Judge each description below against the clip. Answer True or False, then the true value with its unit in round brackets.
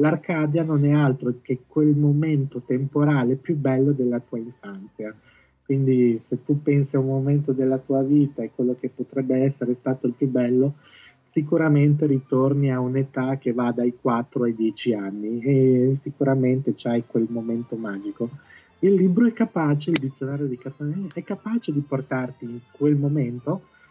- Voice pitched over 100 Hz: True (135 Hz)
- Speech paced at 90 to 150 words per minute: False (160 wpm)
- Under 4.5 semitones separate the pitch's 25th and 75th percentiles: True (2.9 semitones)